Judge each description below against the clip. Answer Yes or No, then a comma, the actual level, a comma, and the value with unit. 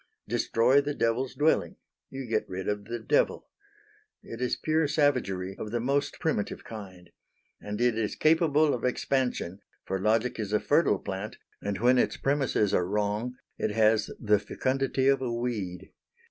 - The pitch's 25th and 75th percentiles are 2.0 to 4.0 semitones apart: No, average, 4.7 semitones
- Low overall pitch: Yes, low, 115 Hz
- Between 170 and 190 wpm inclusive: No, average, 160 wpm